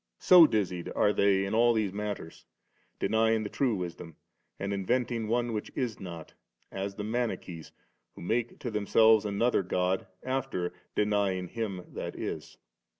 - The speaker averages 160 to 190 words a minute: No, average, 150 wpm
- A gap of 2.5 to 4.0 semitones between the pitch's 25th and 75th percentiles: Yes, average, 3.3 semitones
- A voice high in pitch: No, low, 105 Hz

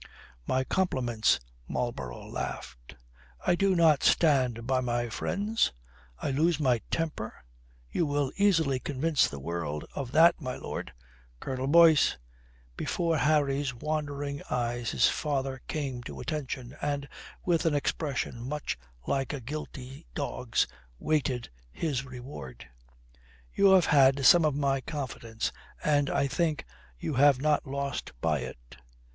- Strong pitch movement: No, average, 3.7 semitones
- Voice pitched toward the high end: No, medium, 140 Hz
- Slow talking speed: Yes, slow, 130 wpm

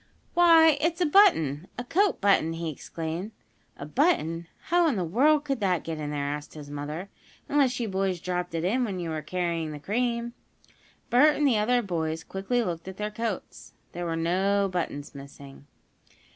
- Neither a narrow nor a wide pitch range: No, wide, 7.2 semitones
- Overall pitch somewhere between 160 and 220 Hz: Yes, medium, 185 Hz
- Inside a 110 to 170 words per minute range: No, average, 185 wpm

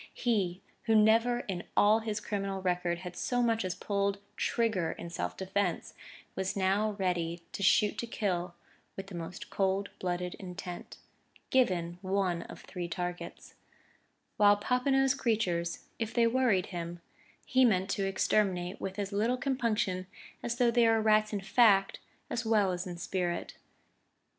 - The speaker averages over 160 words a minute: No, average, 155 wpm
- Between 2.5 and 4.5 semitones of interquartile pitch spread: Yes, average, 3.7 semitones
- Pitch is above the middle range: Yes, high, 195 Hz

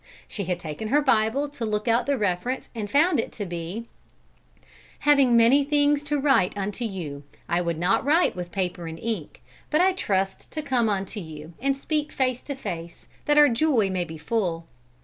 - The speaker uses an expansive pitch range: Yes, wide, 7.7 semitones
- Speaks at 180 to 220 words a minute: Yes, average, 190 wpm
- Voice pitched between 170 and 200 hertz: No, high, 220 Hz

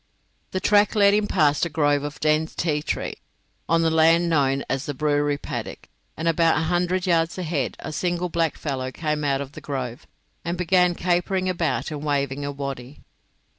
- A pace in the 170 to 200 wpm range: Yes, average, 185 wpm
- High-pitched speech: No, medium, 160 Hz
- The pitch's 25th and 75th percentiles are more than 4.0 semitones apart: No, average, 3.4 semitones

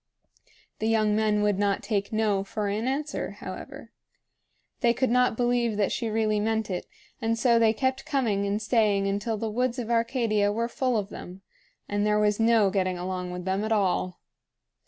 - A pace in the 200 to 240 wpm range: No, average, 185 wpm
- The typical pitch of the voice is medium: No, high, 215 Hz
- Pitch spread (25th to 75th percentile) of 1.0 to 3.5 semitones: Yes, narrow, 2.4 semitones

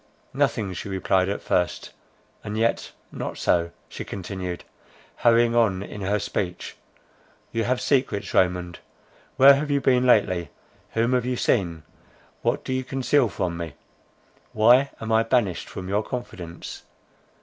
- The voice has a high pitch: No, low, 105 Hz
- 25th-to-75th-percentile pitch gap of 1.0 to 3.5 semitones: No, average, 5.2 semitones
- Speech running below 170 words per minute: Yes, average, 140 wpm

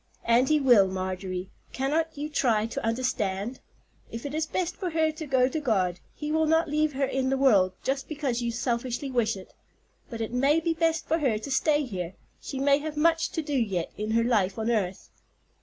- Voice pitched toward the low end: No, very high, 260 Hz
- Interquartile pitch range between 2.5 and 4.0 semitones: No, wide, 5.5 semitones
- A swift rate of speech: Yes, fast, 210 wpm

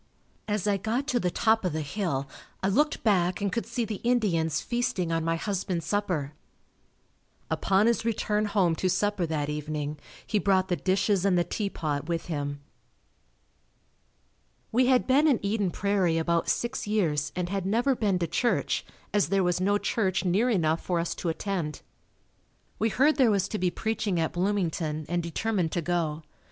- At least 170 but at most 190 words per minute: Yes, average, 175 wpm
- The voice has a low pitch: No, high, 190 Hz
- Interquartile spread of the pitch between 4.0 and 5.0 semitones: Yes, average, 4.3 semitones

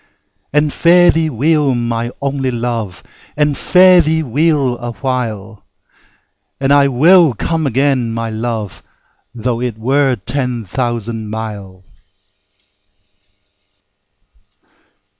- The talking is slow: Yes, slow, 105 wpm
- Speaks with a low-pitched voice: Yes, low, 125 Hz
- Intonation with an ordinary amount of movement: Yes, average, 4.2 semitones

